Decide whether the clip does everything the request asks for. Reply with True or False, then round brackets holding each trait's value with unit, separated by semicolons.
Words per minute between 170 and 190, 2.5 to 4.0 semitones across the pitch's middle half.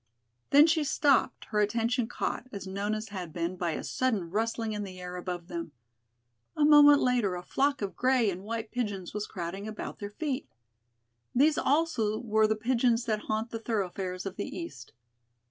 False (180 wpm; 4.7 semitones)